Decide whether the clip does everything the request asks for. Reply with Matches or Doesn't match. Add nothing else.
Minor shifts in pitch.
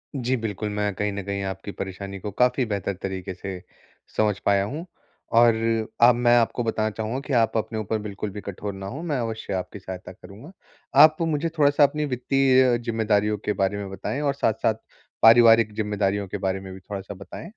Doesn't match